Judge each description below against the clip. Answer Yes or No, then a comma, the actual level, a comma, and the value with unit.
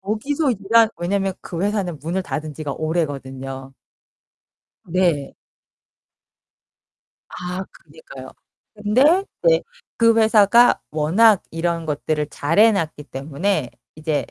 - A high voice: No, medium, 175 Hz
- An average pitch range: No, wide, 5.9 semitones